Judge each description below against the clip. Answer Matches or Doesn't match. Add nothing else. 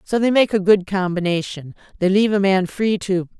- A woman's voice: Matches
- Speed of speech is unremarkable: Doesn't match